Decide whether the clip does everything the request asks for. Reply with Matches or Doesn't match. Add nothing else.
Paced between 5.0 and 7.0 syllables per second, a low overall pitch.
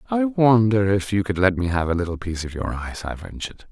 Matches